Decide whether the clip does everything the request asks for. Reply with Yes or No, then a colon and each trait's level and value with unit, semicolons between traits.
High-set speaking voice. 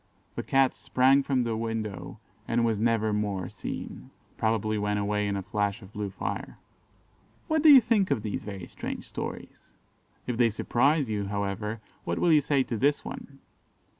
No: low, 110 Hz